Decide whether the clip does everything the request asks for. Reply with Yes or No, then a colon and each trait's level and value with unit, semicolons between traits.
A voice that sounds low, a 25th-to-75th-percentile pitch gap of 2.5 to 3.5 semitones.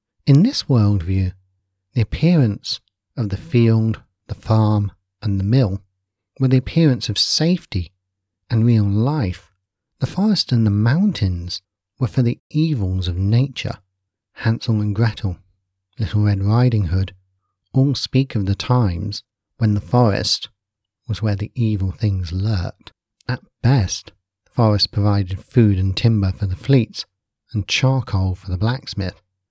No: low, 105 Hz; average, 4.0 semitones